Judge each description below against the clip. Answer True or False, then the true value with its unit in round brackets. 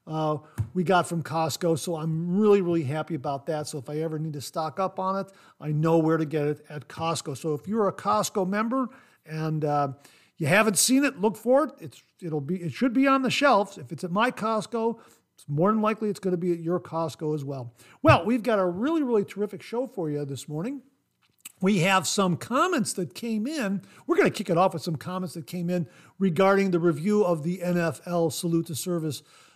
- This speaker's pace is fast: True (225 wpm)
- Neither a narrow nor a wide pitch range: True (4.8 semitones)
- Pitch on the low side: False (175 Hz)